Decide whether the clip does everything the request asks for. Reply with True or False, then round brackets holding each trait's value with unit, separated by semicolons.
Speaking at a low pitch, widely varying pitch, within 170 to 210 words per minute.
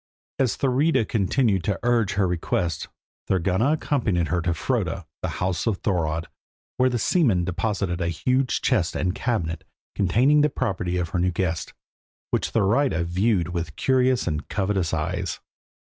False (95 Hz; 6.0 semitones; 150 wpm)